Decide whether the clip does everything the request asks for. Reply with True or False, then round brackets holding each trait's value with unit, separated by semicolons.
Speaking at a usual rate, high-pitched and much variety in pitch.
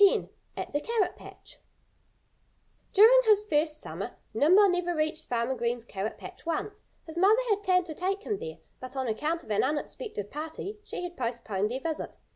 True (180 wpm; 325 Hz; 7.5 semitones)